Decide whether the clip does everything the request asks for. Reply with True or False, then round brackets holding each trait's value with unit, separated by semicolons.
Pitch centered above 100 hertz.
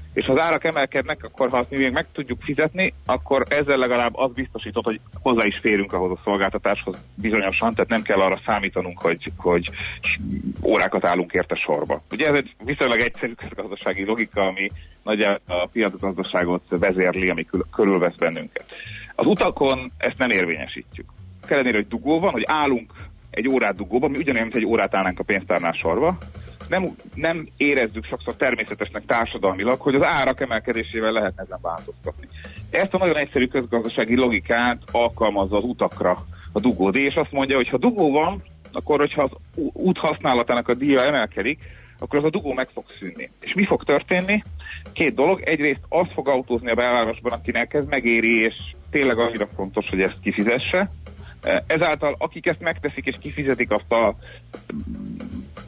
True (115 Hz)